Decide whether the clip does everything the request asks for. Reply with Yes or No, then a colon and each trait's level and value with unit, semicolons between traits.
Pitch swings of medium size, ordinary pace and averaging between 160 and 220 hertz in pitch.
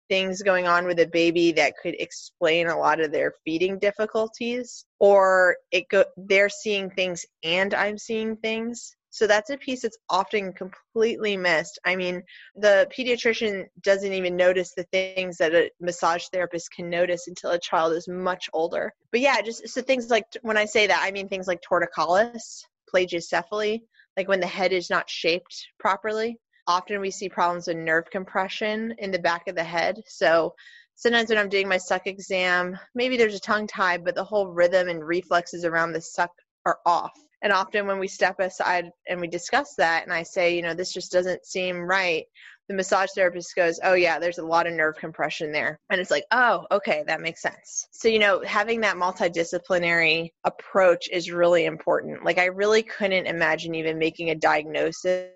Yes: average, 3.3 semitones; average, 190 wpm; medium, 185 Hz